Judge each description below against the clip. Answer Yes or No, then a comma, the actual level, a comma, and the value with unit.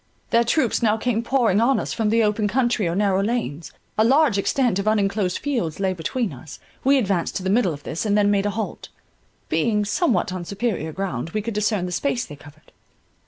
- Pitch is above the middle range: Yes, high, 210 Hz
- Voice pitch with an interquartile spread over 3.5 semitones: Yes, average, 3.9 semitones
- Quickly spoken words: Yes, fast, 210 wpm